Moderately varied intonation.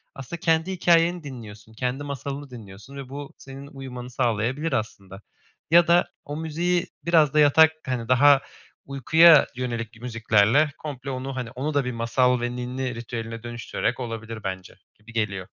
Yes: average, 4.0 semitones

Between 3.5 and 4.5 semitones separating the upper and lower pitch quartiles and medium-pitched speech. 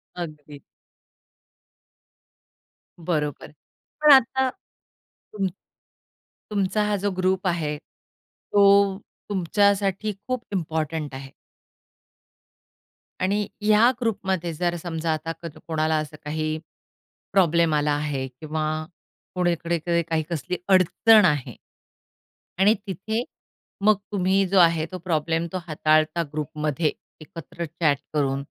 Yes: average, 4.1 semitones; medium, 170 Hz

